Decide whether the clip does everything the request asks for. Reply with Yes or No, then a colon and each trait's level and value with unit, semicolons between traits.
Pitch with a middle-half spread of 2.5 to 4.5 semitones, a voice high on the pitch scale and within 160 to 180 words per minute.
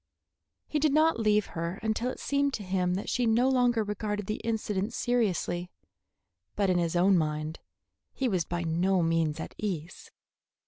No: average, 5.0 semitones; high, 200 Hz; average, 170 wpm